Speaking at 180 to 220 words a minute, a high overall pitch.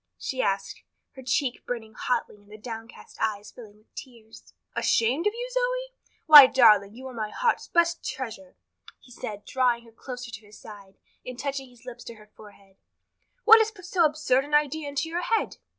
Yes: average, 190 wpm; very high, 250 Hz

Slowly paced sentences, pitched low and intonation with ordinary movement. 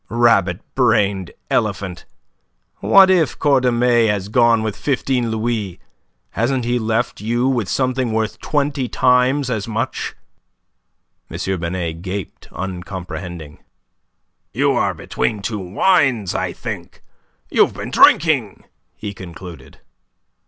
Yes: slow, 110 wpm; low, 115 Hz; average, 4.7 semitones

